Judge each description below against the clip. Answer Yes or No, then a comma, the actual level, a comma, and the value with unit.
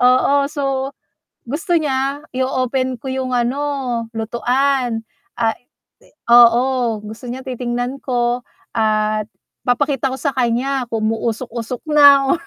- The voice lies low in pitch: No, very high, 250 Hz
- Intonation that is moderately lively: No, narrow, 2.3 semitones